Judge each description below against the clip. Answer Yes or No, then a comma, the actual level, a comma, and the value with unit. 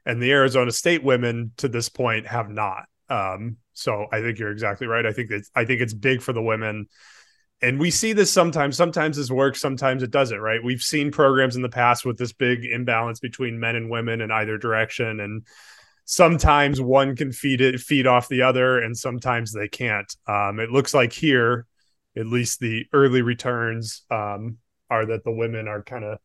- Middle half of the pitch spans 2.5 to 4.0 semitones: Yes, average, 2.9 semitones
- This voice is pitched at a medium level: No, low, 120 Hz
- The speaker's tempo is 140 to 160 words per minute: No, average, 200 wpm